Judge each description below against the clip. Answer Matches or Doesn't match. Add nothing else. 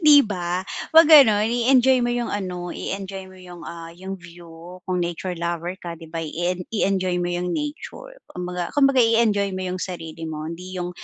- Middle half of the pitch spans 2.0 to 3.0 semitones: Doesn't match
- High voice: Doesn't match